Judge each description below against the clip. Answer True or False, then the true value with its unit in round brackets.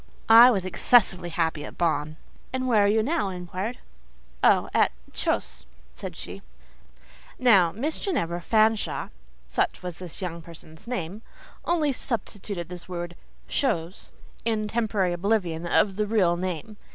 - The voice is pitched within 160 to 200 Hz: True (185 Hz)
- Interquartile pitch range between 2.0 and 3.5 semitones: False (4.4 semitones)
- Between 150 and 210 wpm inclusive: False (140 wpm)